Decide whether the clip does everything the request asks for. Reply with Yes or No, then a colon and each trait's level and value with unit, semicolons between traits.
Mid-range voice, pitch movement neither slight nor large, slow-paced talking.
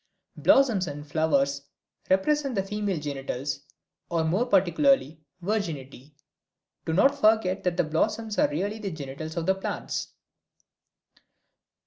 No: medium, 180 Hz; wide, 5.9 semitones; slow, 120 wpm